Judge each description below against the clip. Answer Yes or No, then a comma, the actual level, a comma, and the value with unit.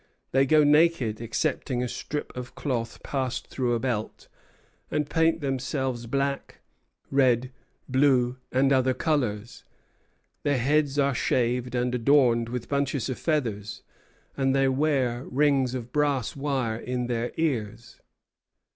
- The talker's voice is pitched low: Yes, low, 130 Hz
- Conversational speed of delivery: No, slow, 130 wpm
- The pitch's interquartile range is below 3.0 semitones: Yes, narrow, 2.6 semitones